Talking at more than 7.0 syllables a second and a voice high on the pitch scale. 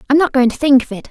Yes: 7.5 syllables/s; very high, 270 Hz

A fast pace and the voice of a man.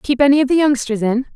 No: fast, 265 wpm; female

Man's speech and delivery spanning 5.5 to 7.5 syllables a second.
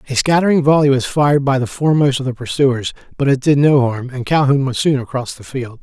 Yes: male; 6.0 syllables/s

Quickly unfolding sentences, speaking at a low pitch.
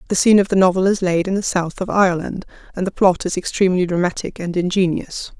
No: fast, 225 wpm; medium, 185 Hz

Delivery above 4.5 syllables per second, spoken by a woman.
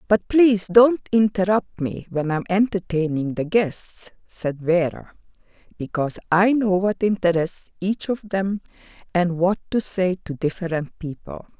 No: 4.4 syllables/s; female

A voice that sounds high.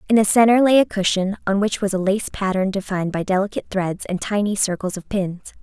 Yes: high, 200 Hz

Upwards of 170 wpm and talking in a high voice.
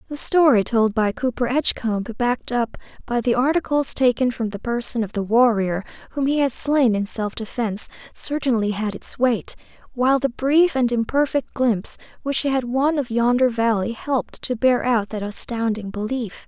Yes: average, 180 wpm; high, 240 Hz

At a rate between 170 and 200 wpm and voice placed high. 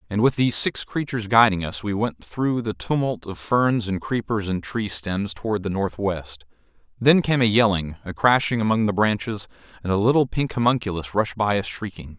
No: average, 195 wpm; low, 105 Hz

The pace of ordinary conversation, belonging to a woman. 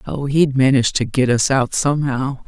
Yes: average, 195 wpm; female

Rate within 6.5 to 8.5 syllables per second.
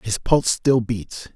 No: 4.0 syllables/s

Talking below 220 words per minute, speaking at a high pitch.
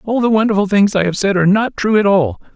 No: fast, 280 wpm; high, 200 Hz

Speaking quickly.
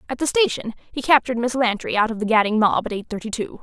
Yes: fast, 265 wpm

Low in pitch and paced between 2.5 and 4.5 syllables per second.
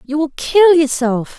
No: very high, 295 Hz; 4.0 syllables/s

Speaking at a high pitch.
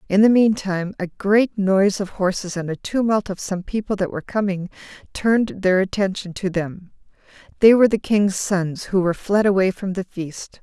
Yes: high, 195 Hz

